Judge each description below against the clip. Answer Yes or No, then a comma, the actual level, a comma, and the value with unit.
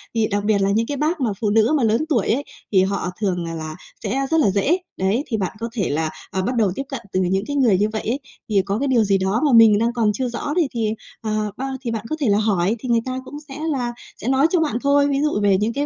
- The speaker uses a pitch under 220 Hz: No, high, 225 Hz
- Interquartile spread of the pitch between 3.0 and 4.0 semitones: No, average, 4.9 semitones